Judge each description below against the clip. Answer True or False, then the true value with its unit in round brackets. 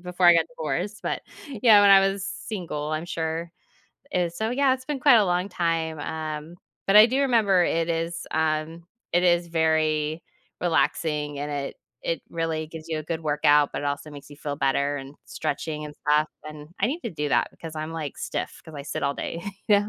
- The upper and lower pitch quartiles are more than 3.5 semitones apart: False (3.2 semitones)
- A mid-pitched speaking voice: True (160 Hz)